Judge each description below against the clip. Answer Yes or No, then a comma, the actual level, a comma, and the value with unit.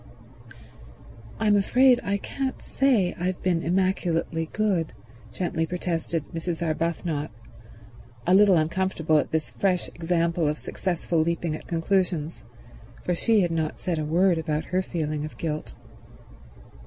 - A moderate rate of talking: No, slow, 130 wpm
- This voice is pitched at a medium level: Yes, medium, 170 Hz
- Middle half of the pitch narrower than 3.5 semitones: Yes, average, 2.7 semitones